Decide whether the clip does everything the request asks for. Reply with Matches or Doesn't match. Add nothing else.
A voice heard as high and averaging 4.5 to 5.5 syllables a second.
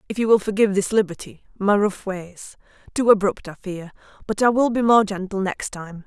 Matches